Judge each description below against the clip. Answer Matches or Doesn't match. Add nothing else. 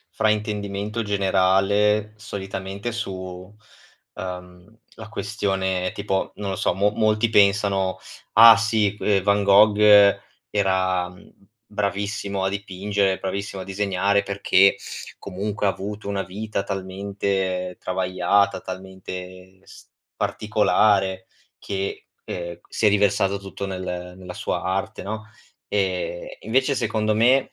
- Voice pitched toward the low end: Matches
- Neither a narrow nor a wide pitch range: Doesn't match